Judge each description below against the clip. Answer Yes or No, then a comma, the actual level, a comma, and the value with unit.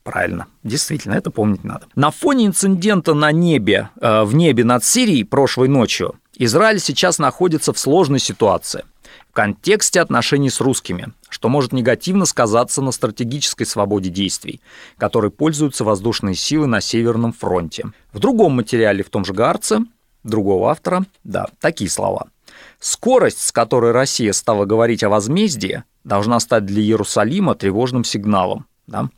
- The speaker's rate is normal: Yes, average, 145 wpm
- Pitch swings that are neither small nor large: No, wide, 6.3 semitones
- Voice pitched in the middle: No, low, 125 Hz